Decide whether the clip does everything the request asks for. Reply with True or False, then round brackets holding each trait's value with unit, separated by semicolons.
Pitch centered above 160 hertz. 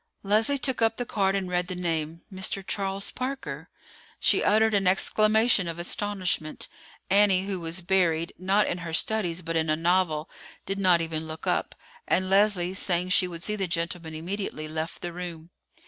True (185 Hz)